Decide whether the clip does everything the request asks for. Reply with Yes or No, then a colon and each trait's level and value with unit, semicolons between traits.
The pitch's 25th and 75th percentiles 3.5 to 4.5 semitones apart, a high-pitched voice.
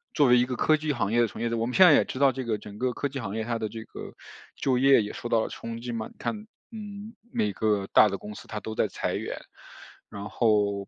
No: average, 4.2 semitones; low, 115 Hz